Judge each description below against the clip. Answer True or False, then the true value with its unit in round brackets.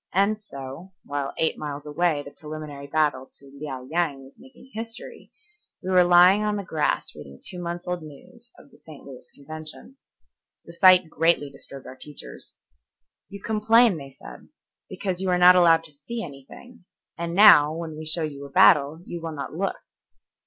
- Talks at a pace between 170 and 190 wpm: True (180 wpm)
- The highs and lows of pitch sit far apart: False (4.5 semitones)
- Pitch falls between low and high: True (165 Hz)